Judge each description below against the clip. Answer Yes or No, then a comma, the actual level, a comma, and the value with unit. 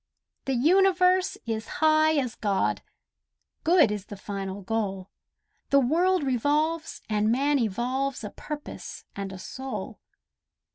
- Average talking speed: No, slow, 125 wpm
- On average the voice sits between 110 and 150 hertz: No, very high, 260 Hz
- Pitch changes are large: Yes, wide, 6.9 semitones